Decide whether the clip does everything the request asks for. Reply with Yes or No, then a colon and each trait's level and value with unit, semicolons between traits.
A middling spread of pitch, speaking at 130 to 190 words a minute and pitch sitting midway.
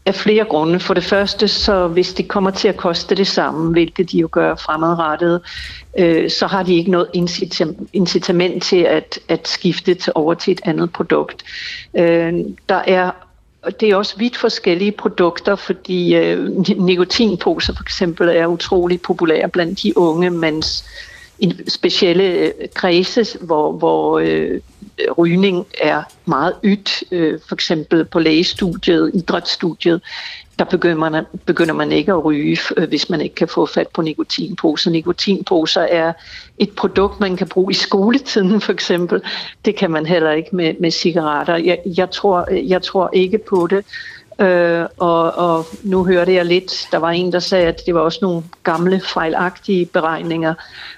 No: narrow, 2.3 semitones; average, 160 wpm; medium, 180 Hz